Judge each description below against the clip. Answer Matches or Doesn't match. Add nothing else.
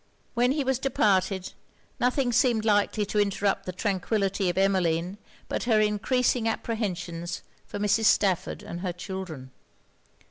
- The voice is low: Doesn't match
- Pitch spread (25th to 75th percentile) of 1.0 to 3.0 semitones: Doesn't match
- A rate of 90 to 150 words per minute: Matches